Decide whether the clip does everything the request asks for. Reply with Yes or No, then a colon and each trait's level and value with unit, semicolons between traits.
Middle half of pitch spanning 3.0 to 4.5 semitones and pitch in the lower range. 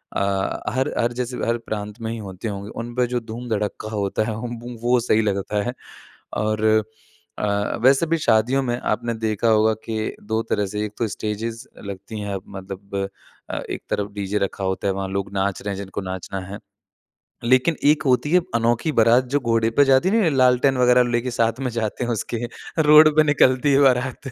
Yes: average, 3.6 semitones; low, 115 Hz